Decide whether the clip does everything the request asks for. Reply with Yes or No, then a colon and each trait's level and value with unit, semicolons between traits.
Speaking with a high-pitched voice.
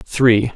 No: low, 120 Hz